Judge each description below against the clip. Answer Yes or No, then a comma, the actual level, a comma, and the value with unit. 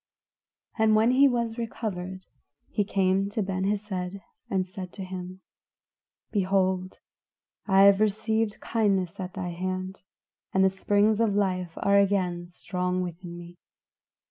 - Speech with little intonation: Yes, narrow, 2.1 semitones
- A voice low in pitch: No, high, 190 Hz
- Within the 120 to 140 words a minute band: Yes, slow, 135 wpm